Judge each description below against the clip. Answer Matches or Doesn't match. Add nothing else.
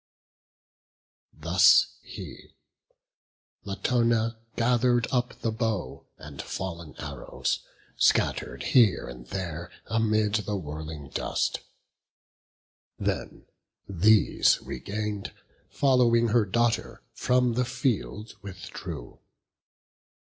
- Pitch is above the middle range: Doesn't match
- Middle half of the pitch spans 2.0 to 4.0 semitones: Doesn't match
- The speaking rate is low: Matches